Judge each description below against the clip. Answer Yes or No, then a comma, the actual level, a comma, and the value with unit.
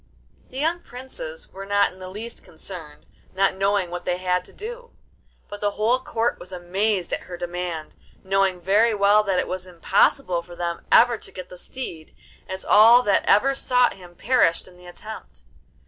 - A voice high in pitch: Yes, high, 195 Hz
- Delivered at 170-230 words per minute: Yes, average, 185 wpm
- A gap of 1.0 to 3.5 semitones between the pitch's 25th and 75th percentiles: No, average, 4.3 semitones